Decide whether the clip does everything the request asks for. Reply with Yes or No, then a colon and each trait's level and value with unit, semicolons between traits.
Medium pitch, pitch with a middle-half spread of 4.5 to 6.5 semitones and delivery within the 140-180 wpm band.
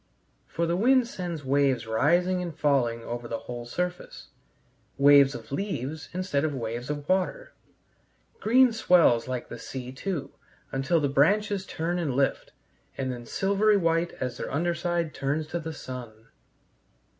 Yes: medium, 150 Hz; wide, 5.6 semitones; average, 155 wpm